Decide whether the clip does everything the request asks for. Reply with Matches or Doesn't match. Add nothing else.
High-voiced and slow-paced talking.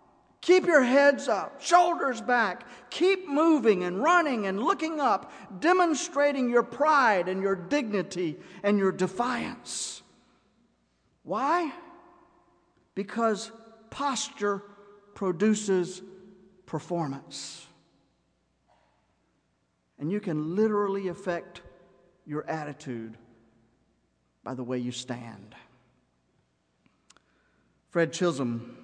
Matches